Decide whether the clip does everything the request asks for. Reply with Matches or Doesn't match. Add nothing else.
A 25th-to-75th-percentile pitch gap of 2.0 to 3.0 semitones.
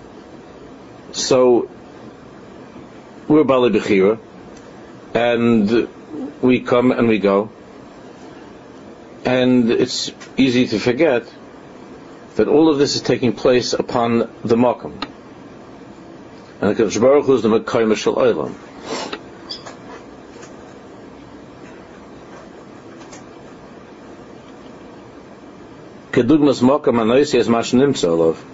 Matches